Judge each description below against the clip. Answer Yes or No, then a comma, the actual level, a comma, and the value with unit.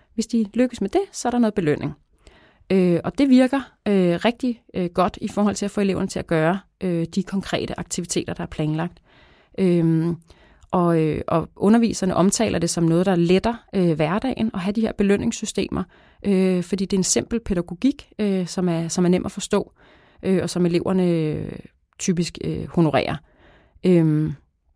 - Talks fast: No, slow, 145 wpm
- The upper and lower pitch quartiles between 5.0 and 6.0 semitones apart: No, average, 3.6 semitones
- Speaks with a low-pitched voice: No, medium, 185 Hz